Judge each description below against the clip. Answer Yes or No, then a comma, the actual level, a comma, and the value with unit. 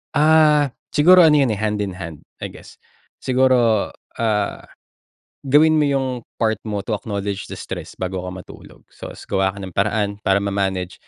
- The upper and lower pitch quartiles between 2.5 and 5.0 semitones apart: No, wide, 5.6 semitones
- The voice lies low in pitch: Yes, low, 105 Hz